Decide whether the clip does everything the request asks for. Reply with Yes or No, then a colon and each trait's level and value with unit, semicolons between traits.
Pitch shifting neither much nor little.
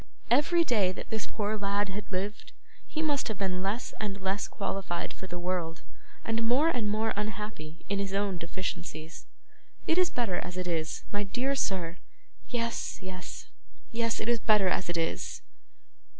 Yes: average, 3.6 semitones